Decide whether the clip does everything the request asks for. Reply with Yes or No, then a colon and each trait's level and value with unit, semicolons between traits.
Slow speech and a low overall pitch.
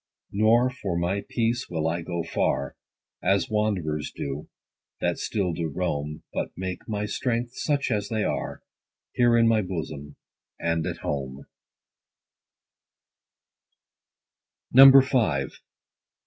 Yes: slow, 110 wpm; very low, 95 Hz